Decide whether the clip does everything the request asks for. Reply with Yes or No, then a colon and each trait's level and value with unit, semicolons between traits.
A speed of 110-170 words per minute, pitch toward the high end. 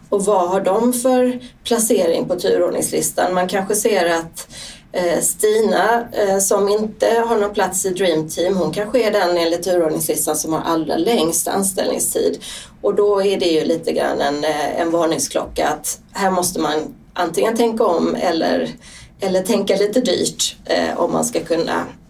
Yes: average, 160 wpm; high, 195 Hz